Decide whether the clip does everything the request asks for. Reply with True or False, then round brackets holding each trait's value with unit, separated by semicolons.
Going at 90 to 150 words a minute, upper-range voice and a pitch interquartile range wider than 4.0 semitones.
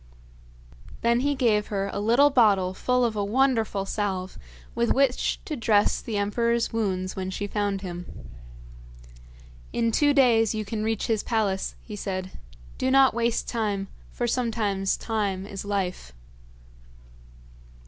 False (140 wpm; 215 Hz; 3.1 semitones)